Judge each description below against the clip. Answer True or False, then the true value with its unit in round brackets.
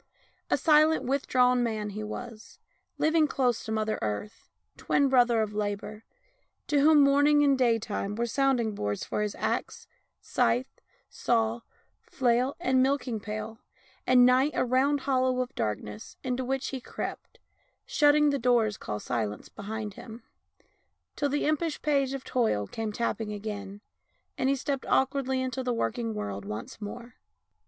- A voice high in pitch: True (245 Hz)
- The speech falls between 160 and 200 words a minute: False (150 wpm)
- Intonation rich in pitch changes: False (4.0 semitones)